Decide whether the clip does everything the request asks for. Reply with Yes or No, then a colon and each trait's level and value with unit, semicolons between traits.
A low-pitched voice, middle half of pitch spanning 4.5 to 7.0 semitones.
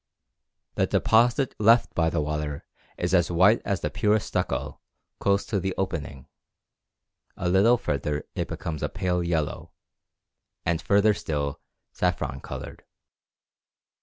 Yes: very low, 90 Hz; average, 5.0 semitones